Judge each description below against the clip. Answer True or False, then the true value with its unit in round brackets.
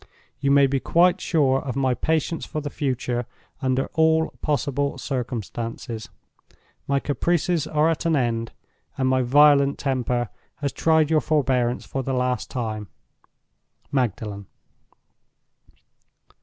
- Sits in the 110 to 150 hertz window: True (135 Hz)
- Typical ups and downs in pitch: True (3.4 semitones)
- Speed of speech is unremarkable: False (125 wpm)